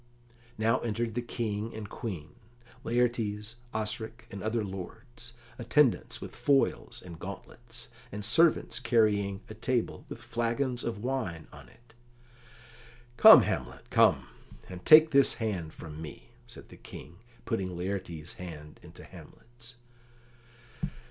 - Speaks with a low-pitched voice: Yes, low, 110 Hz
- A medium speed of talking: No, slow, 125 wpm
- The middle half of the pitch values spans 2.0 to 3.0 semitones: No, average, 3.8 semitones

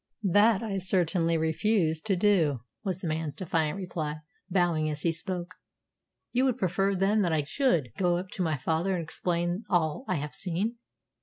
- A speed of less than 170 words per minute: No, average, 175 wpm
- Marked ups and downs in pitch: No, average, 3.4 semitones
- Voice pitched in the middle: Yes, medium, 175 Hz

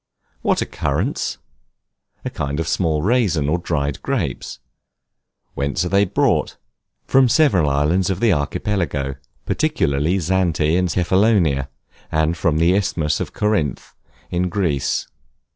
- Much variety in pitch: No, average, 4.3 semitones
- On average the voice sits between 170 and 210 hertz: No, very low, 85 Hz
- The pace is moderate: No, slow, 125 wpm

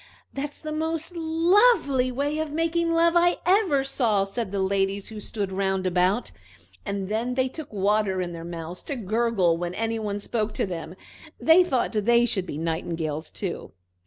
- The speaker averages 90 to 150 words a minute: No, average, 175 wpm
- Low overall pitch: No, high, 220 Hz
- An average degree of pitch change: No, wide, 7.7 semitones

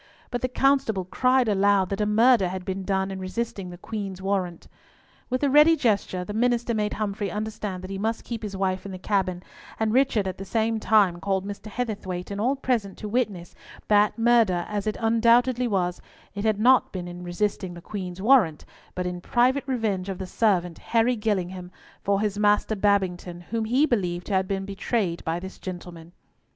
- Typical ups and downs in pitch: Yes, average, 3.4 semitones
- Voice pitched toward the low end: No, high, 200 Hz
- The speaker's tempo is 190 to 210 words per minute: Yes, average, 195 wpm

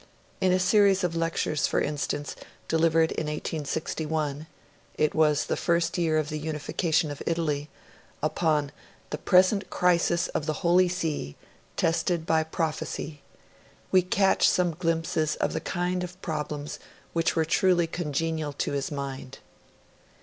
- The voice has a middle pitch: Yes, medium, 160 Hz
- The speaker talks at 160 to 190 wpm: No, average, 140 wpm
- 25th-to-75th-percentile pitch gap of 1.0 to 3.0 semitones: Yes, narrow, 2.5 semitones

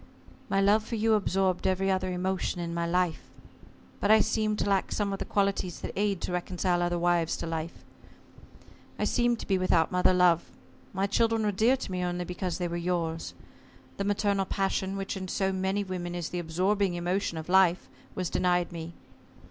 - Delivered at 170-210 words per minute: Yes, average, 195 wpm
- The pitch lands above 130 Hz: Yes, medium, 185 Hz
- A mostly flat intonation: Yes, narrow, 2.2 semitones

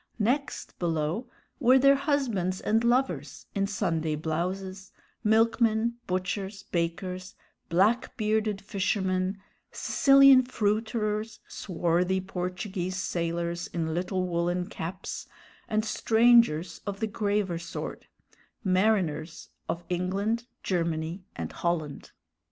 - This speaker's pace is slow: Yes, slow, 100 wpm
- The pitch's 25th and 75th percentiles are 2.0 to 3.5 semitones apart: No, average, 4.1 semitones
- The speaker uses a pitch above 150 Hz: Yes, high, 190 Hz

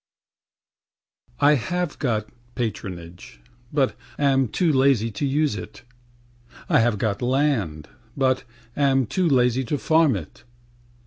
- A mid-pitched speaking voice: No, low, 130 Hz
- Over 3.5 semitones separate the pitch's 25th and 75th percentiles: Yes, average, 4.7 semitones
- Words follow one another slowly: Yes, slow, 125 wpm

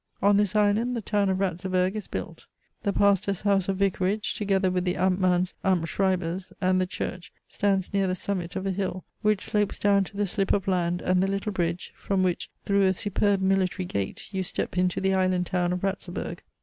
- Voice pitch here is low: No, high, 190 Hz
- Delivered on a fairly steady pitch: Yes, narrow, 1.6 semitones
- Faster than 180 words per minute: Yes, average, 200 wpm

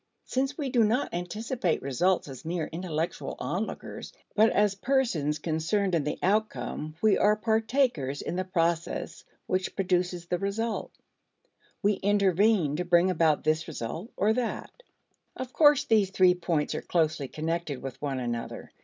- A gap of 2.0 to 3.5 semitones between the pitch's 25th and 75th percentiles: No, average, 5.3 semitones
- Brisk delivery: No, average, 150 wpm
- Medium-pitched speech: Yes, medium, 180 Hz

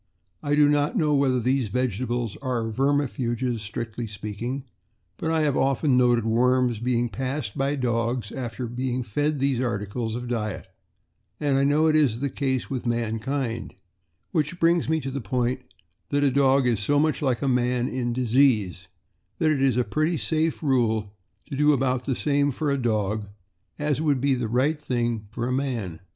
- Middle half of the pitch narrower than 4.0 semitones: Yes, average, 3.3 semitones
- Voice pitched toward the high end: No, low, 130 Hz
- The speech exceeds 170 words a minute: Yes, average, 180 wpm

